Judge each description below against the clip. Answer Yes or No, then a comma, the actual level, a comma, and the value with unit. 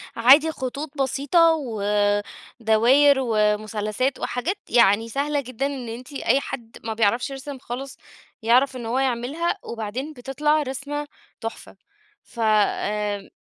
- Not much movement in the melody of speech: No, average, 4.0 semitones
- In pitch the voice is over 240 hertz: Yes, very high, 250 Hz